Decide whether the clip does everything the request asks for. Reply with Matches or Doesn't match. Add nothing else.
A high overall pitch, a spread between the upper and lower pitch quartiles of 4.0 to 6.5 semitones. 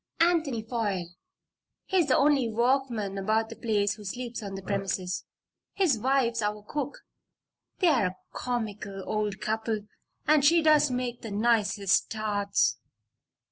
Matches